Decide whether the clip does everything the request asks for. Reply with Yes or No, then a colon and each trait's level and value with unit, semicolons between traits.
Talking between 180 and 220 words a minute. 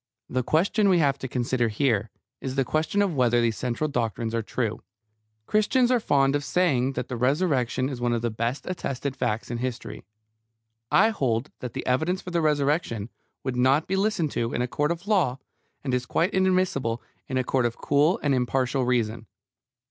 Yes: average, 195 wpm